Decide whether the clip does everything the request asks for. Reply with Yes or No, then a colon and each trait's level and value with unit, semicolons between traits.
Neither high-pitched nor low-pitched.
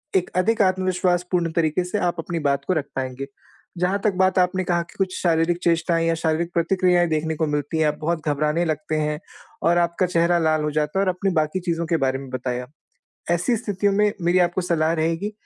Yes: medium, 170 Hz